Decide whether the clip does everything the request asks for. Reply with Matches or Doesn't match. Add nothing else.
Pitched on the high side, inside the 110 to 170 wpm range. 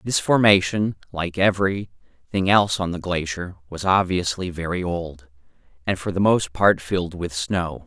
Doesn't match